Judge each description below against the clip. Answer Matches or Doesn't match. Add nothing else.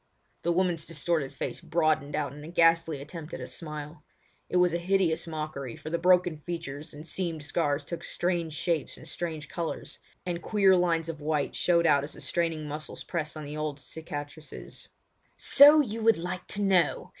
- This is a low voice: Doesn't match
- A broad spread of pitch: Doesn't match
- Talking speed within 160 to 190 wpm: Matches